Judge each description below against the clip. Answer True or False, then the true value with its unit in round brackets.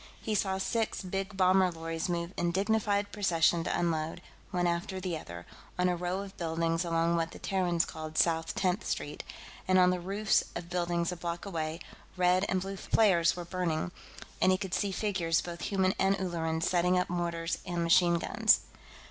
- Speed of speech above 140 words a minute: True (185 wpm)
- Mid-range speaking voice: True (175 Hz)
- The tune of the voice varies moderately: False (2.2 semitones)